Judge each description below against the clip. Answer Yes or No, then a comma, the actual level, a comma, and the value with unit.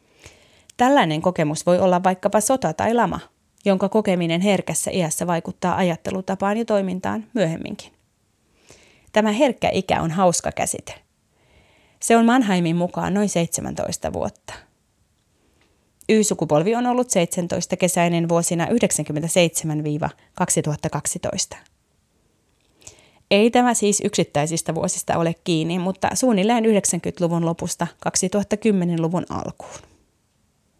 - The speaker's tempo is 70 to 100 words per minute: Yes, slow, 95 wpm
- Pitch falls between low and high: Yes, medium, 180 Hz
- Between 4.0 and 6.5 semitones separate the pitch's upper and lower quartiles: No, average, 3.6 semitones